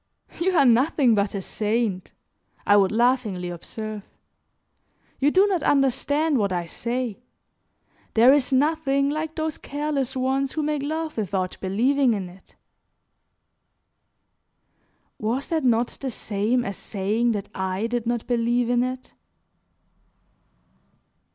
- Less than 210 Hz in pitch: No, high, 245 Hz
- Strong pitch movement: No, average, 4.9 semitones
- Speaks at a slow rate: Yes, slow, 125 wpm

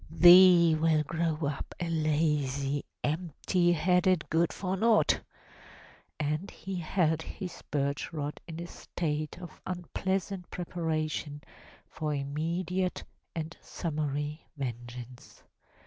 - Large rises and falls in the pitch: No, average, 3.1 semitones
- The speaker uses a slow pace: Yes, slow, 110 wpm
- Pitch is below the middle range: No, medium, 160 Hz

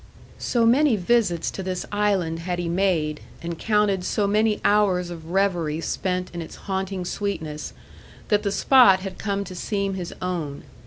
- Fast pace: No, average, 165 wpm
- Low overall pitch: No, high, 190 Hz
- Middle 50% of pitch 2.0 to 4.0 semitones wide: Yes, average, 3.0 semitones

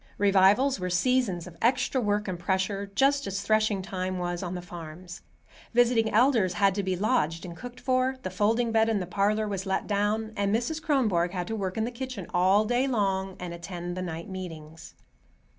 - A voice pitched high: Yes, high, 200 Hz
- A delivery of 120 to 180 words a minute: No, average, 195 wpm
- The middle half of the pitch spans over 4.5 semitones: No, average, 3.8 semitones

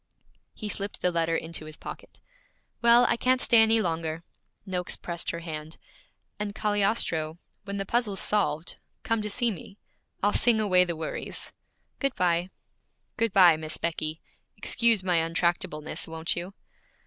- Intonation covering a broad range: No, average, 4.4 semitones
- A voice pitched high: No, medium, 180 Hz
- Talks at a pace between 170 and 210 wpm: No, average, 150 wpm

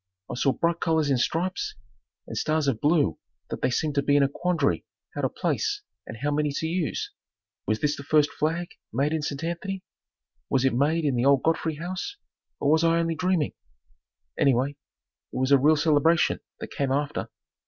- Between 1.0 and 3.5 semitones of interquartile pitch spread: Yes, average, 3.0 semitones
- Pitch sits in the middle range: Yes, medium, 150 Hz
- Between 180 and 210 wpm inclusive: Yes, average, 195 wpm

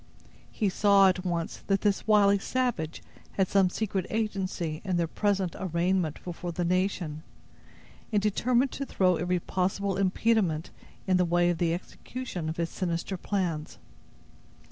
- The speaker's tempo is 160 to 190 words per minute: No, average, 145 wpm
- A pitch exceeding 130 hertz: Yes, medium, 185 Hz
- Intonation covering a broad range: No, average, 2.7 semitones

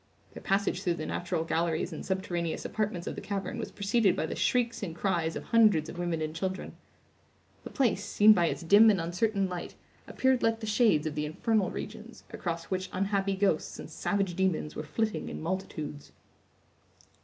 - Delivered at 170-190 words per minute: Yes, average, 185 wpm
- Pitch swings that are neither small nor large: Yes, average, 3.8 semitones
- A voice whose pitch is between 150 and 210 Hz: Yes, high, 190 Hz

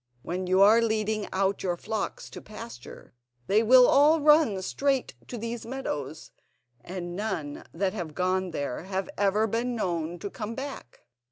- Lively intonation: No, average, 4.3 semitones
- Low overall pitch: No, high, 200 Hz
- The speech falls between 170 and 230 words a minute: No, average, 160 wpm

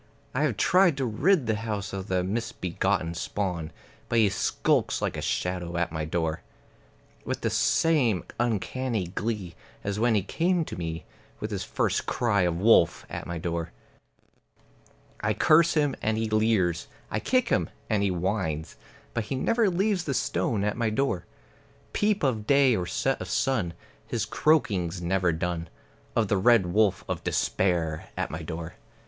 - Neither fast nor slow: Yes, average, 165 wpm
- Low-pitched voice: Yes, low, 105 Hz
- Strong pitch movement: Yes, wide, 6.0 semitones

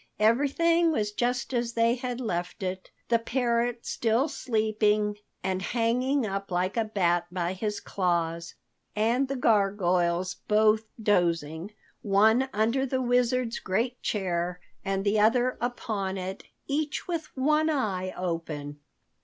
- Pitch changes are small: No, average, 4.9 semitones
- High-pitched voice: Yes, high, 215 Hz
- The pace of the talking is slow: Yes, slow, 130 wpm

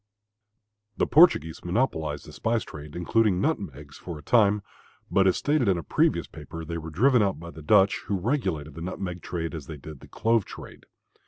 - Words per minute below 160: No, average, 190 wpm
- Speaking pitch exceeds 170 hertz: No, very low, 90 Hz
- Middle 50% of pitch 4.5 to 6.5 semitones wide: Yes, wide, 5.4 semitones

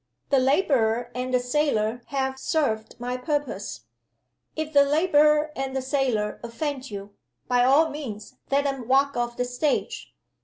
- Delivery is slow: No, average, 150 wpm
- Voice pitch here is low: No, very high, 265 Hz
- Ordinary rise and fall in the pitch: Yes, average, 3.2 semitones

